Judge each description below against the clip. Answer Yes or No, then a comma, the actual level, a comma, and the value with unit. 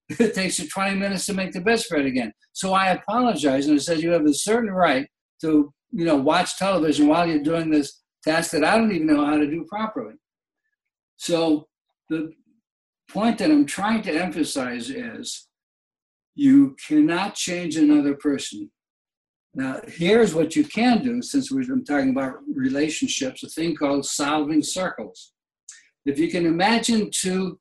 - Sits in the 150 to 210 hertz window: Yes, medium, 185 Hz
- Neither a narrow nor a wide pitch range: No, wide, 7.9 semitones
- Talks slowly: No, average, 165 wpm